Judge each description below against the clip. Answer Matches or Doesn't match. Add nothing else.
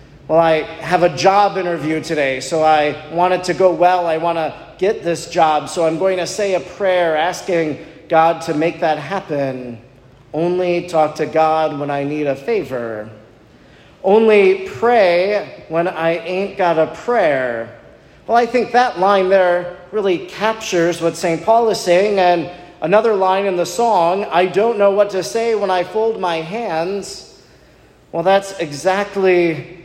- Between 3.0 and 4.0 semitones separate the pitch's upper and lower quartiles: Matches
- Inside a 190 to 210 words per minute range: Doesn't match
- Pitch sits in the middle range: Matches